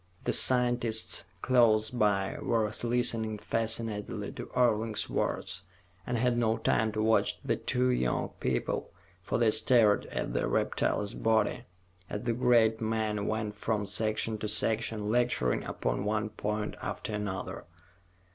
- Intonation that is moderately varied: No, narrow, 1.9 semitones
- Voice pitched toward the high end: No, low, 110 Hz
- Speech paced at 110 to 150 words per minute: Yes, slow, 135 wpm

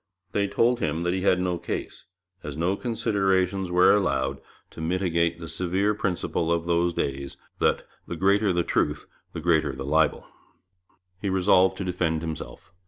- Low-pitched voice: Yes, very low, 90 Hz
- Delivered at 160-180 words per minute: Yes, average, 165 wpm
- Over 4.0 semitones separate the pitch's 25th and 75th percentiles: No, average, 2.9 semitones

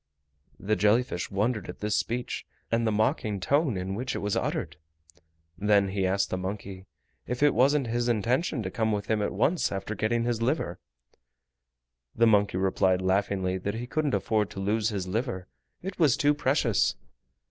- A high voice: No, low, 105 Hz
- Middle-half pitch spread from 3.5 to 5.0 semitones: Yes, average, 3.8 semitones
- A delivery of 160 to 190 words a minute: Yes, average, 180 wpm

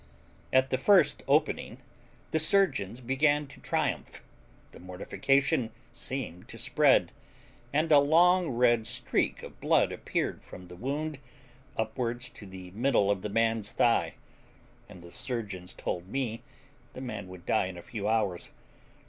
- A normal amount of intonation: No, wide, 5.8 semitones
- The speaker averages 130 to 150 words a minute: Yes, average, 145 wpm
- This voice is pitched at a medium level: No, low, 120 Hz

